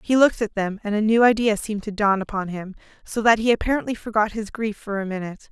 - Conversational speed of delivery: No, fast, 250 wpm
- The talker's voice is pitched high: Yes, high, 210 Hz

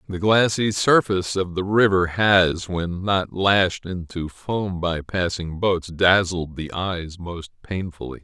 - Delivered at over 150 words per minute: No, average, 145 wpm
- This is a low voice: Yes, very low, 90 Hz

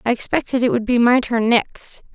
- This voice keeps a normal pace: No, fast, 225 wpm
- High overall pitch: Yes, high, 240 Hz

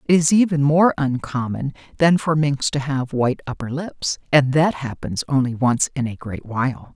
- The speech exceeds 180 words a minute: Yes, average, 190 wpm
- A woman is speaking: Yes, female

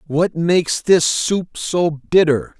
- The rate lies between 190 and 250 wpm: No, average, 140 wpm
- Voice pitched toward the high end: No, medium, 165 Hz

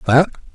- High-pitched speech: No, medium, 140 Hz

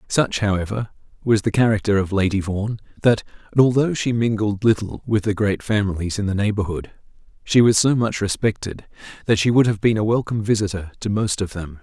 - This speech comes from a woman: No, male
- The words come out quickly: No, average, 190 wpm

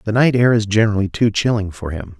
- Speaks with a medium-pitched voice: No, low, 105 Hz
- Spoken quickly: Yes, fast, 245 wpm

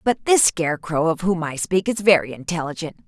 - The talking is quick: No, average, 195 wpm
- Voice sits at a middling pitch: Yes, medium, 170 Hz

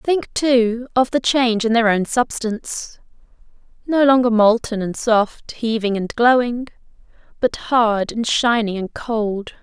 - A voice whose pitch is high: Yes, high, 230 Hz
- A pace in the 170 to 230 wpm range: No, slow, 135 wpm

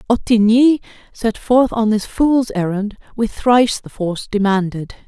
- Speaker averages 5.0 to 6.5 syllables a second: No, 4.5 syllables/s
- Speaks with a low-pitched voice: No, high, 220 Hz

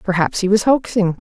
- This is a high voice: Yes, high, 200 Hz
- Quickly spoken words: No, average, 190 wpm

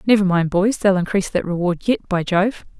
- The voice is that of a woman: Yes, female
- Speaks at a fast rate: Yes, fast, 215 wpm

